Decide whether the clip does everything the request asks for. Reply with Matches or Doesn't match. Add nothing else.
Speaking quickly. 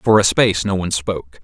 Matches